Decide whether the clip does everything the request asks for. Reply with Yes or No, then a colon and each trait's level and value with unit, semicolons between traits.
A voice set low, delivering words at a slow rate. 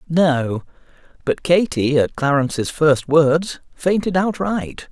No: medium, 155 Hz; slow, 110 wpm